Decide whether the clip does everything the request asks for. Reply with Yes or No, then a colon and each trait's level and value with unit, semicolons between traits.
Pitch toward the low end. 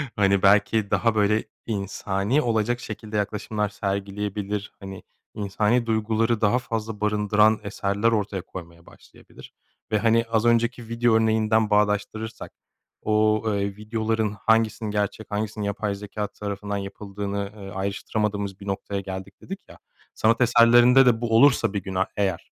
Yes: low, 105 Hz